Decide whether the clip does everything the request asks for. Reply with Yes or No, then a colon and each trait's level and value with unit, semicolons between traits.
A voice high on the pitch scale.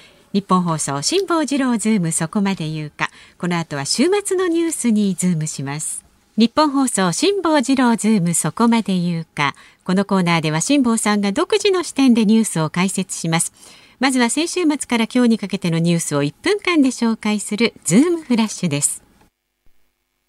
Yes: high, 215 Hz